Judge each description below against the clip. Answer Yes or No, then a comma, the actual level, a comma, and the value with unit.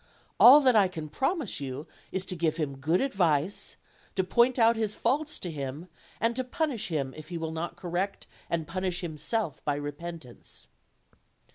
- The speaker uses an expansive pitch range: Yes, wide, 6.7 semitones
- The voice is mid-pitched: Yes, medium, 175 Hz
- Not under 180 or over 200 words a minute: No, average, 170 wpm